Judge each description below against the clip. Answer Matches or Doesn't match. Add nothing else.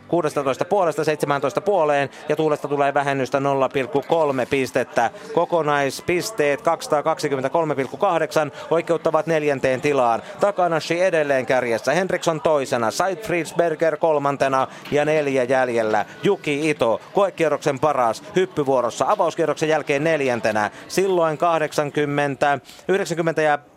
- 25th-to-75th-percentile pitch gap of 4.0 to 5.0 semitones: Doesn't match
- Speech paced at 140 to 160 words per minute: Doesn't match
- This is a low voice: Doesn't match